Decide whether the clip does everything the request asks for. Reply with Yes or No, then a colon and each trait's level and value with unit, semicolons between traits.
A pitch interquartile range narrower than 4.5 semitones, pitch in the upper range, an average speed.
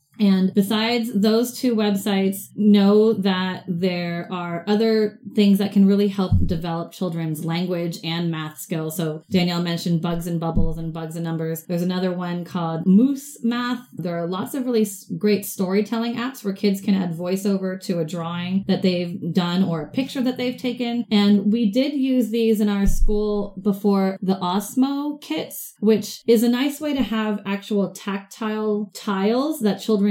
Yes: average, 3.7 semitones; high, 200 Hz; average, 170 wpm